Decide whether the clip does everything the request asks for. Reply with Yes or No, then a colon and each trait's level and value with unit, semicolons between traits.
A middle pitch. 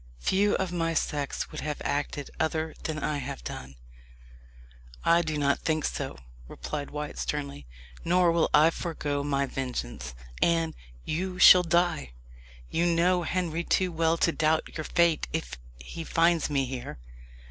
Yes: medium, 160 Hz